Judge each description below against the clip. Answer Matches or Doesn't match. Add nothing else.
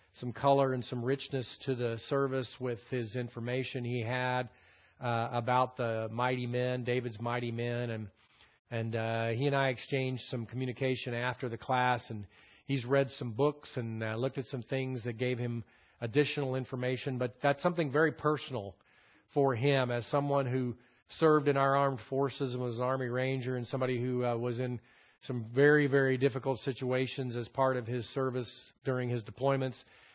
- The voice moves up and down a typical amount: Doesn't match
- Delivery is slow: Doesn't match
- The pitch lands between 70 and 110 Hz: Doesn't match